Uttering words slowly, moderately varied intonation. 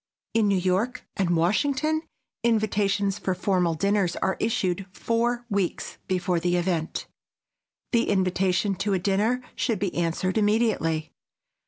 Yes: slow, 130 wpm; average, 3.5 semitones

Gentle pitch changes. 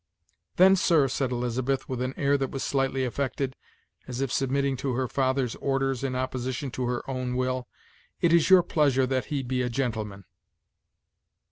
Yes: narrow, 1.4 semitones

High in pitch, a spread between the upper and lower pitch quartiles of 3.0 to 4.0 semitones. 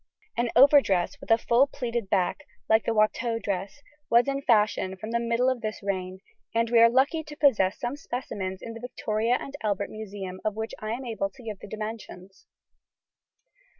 Yes: high, 225 Hz; average, 3.4 semitones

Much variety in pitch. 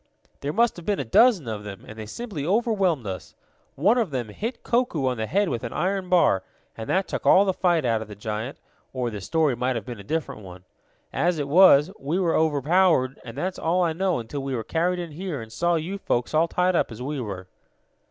Yes: wide, 7.6 semitones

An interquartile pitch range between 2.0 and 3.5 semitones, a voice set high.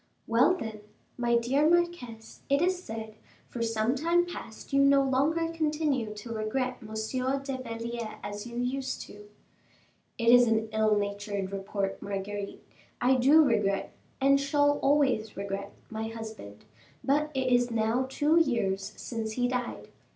No: average, 4.2 semitones; high, 240 Hz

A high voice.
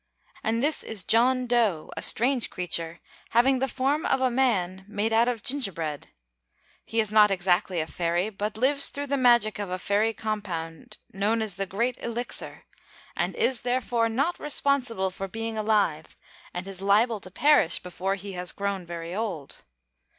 Yes: high, 215 Hz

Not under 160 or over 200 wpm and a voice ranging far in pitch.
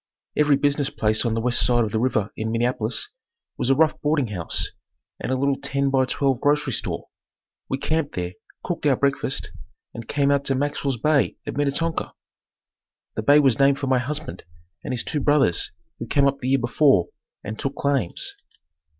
No: average, 190 wpm; average, 3.2 semitones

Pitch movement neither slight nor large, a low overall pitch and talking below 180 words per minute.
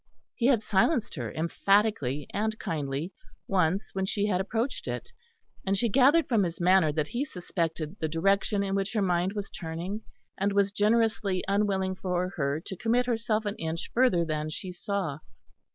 No: average, 4.1 semitones; high, 195 Hz; average, 170 wpm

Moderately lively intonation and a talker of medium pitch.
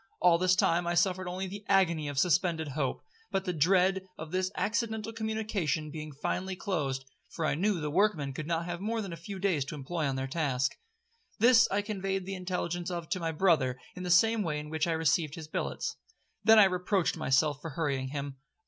Yes: average, 4.1 semitones; medium, 175 Hz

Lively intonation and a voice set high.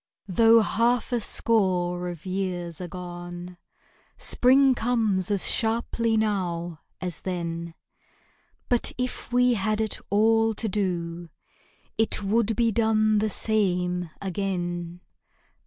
No: average, 4.1 semitones; high, 195 Hz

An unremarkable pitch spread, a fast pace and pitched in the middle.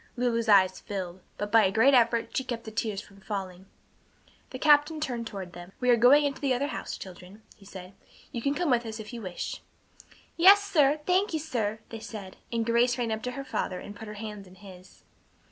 No: average, 4.7 semitones; fast, 215 wpm; high, 225 Hz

